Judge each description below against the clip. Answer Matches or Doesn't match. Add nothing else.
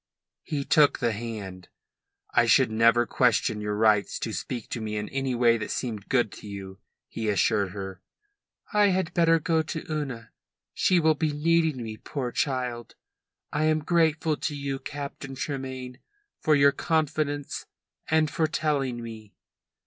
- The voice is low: Matches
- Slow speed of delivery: Doesn't match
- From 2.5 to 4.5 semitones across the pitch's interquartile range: Doesn't match